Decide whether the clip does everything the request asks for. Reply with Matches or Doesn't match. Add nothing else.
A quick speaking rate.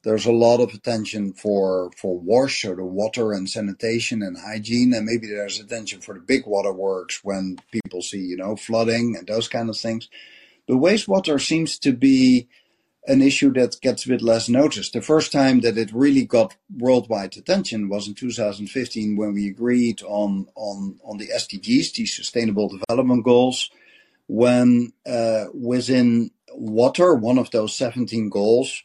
Doesn't match